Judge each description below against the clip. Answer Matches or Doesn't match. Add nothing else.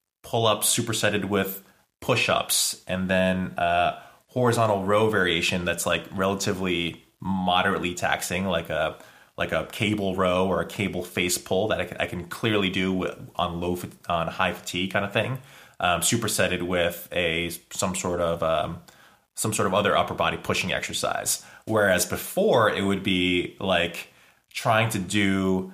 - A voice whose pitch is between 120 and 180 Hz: Doesn't match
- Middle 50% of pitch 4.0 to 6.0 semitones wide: Doesn't match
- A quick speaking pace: Doesn't match